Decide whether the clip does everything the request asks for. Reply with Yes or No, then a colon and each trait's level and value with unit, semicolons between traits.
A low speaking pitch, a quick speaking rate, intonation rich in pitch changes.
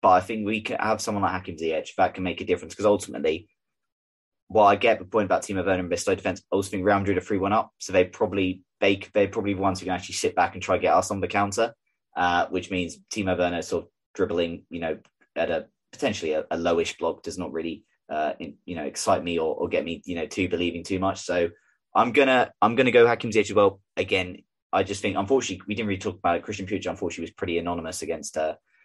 No: very low, 95 Hz; fast, 260 wpm; narrow, 2.5 semitones